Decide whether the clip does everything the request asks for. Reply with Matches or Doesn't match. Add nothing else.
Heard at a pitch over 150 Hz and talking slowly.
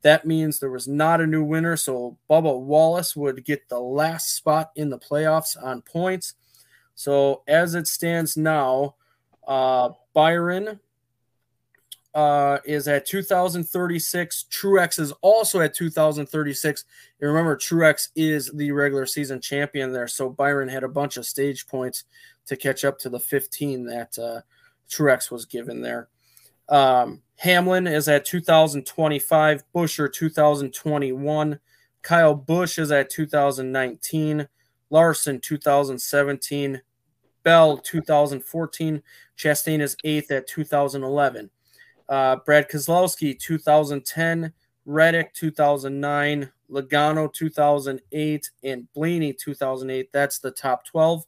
Doesn't match